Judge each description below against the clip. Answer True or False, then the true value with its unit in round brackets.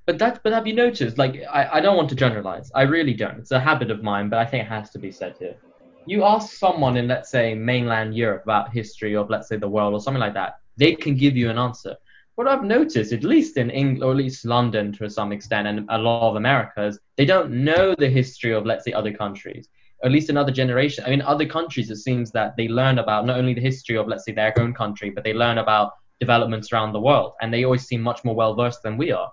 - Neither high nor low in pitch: False (120 Hz)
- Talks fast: True (260 wpm)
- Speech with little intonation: False (4.0 semitones)